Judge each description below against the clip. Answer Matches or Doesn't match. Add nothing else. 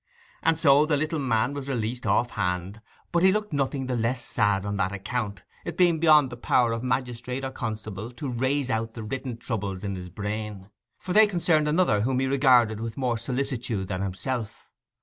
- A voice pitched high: Doesn't match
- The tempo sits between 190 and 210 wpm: Matches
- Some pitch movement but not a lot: Matches